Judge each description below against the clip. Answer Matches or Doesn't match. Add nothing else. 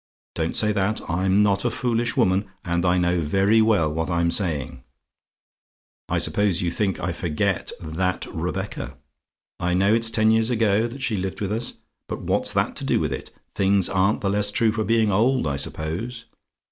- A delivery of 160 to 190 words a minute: Matches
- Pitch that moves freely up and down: Doesn't match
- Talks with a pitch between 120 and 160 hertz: Doesn't match